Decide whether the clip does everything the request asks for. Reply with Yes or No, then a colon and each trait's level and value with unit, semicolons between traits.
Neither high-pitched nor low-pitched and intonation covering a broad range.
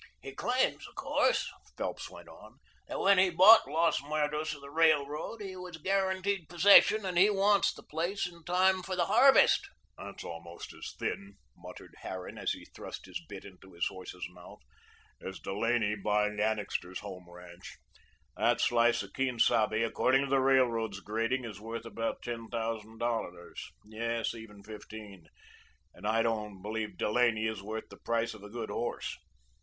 No: low, 115 Hz; wide, 7.7 semitones